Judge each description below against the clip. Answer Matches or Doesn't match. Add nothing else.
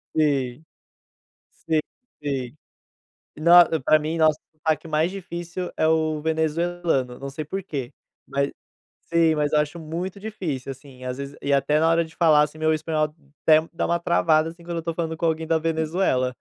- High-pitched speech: Doesn't match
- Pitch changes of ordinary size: Doesn't match